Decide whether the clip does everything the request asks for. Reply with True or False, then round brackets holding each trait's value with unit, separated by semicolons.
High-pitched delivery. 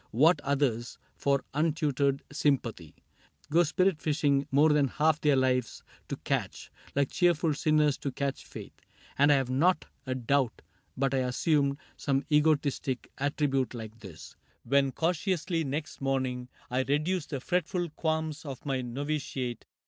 False (140 Hz)